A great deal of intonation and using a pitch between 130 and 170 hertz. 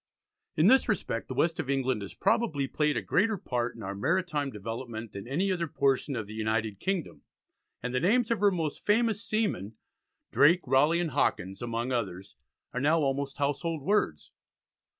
Yes: wide, 7.1 semitones; medium, 140 Hz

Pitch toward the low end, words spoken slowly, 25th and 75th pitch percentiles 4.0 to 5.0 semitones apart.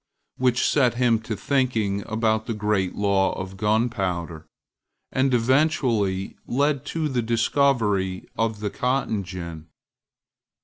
Yes: low, 110 Hz; slow, 120 wpm; average, 4.4 semitones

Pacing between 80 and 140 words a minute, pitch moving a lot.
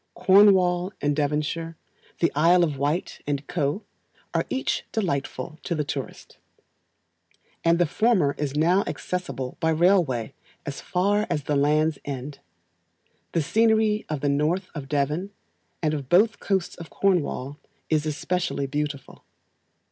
No: slow, 135 wpm; average, 4.0 semitones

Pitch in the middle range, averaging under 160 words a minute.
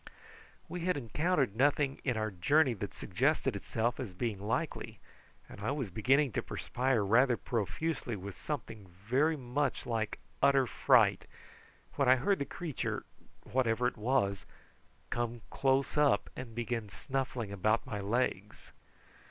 No: low, 120 Hz; average, 140 wpm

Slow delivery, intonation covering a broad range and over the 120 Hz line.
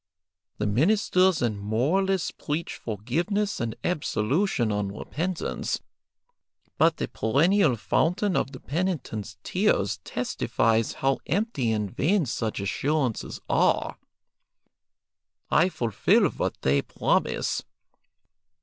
Yes: slow, 100 wpm; wide, 8.7 semitones; low, 135 Hz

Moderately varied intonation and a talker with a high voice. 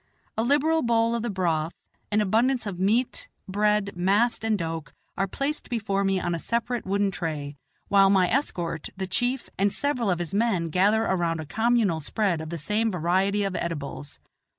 Yes: average, 4.7 semitones; high, 200 Hz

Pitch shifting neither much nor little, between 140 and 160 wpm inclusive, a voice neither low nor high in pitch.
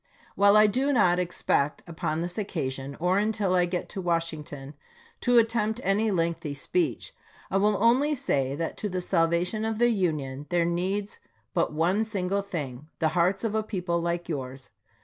No: average, 4.4 semitones; average, 175 wpm; medium, 180 Hz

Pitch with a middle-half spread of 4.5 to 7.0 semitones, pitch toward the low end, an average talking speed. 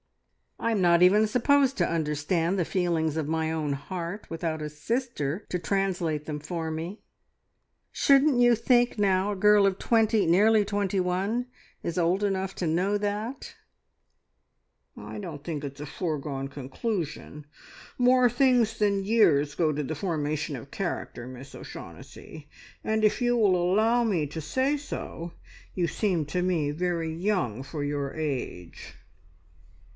No: wide, 5.4 semitones; medium, 180 Hz; average, 150 wpm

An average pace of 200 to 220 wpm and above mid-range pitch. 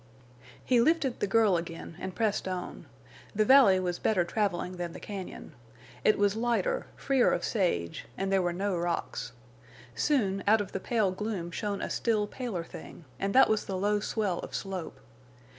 No: average, 175 wpm; high, 200 Hz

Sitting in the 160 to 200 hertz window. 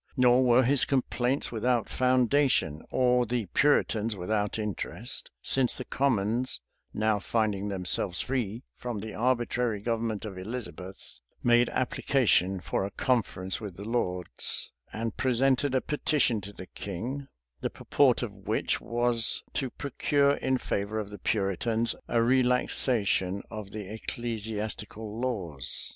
No: low, 115 Hz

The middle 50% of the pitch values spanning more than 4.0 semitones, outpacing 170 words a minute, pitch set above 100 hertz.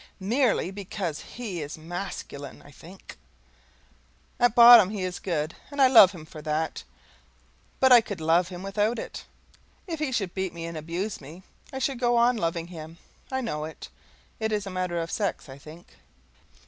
Yes: wide, 5.5 semitones; average, 180 wpm; medium, 185 Hz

